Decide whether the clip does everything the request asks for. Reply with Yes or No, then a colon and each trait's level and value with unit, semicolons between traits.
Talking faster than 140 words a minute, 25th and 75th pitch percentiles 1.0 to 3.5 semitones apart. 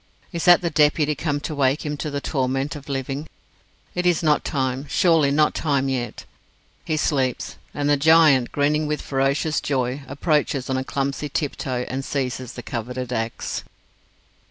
Yes: average, 160 wpm; narrow, 2.4 semitones